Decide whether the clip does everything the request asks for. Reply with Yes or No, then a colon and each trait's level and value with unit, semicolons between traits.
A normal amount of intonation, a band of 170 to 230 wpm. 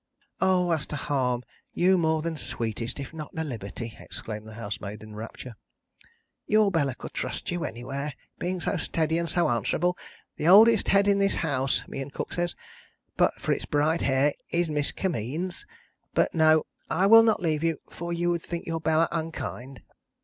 Yes: average, 4.7 semitones; average, 185 wpm